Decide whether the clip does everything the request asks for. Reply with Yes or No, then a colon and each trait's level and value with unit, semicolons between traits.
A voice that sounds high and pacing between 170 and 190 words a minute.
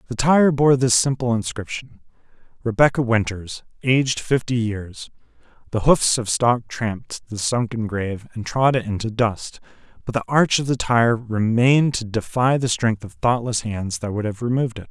No: low, 115 Hz; average, 175 wpm